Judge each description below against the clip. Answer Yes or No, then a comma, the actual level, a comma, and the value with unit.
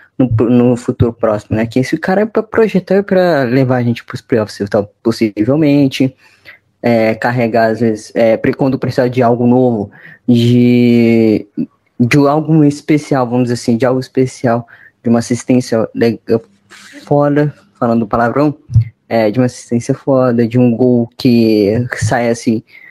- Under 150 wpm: No, average, 155 wpm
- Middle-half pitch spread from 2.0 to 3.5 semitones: Yes, narrow, 2.4 semitones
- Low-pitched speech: Yes, low, 120 Hz